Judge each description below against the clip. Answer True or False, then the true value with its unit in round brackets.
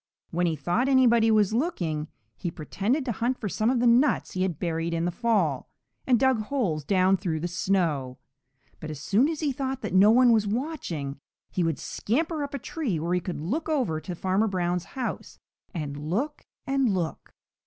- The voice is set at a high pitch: True (195 Hz)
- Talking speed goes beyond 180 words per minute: True (195 wpm)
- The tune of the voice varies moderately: False (7.1 semitones)